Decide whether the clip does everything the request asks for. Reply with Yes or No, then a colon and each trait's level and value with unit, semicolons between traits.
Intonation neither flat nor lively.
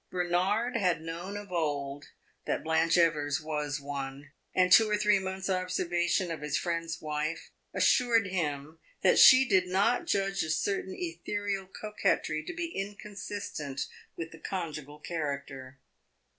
Yes: average, 4.5 semitones